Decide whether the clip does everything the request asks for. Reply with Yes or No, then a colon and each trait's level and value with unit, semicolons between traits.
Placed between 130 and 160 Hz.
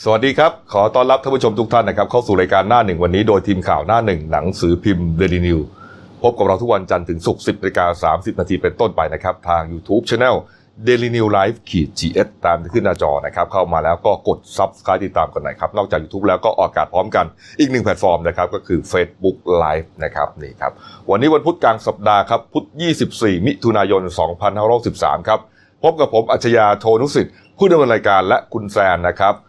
No: low, 100 Hz